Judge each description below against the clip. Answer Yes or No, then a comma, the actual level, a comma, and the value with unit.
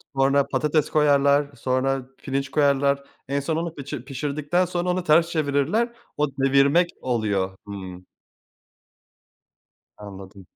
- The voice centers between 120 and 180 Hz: Yes, medium, 140 Hz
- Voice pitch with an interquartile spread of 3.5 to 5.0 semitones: No, narrow, 2.6 semitones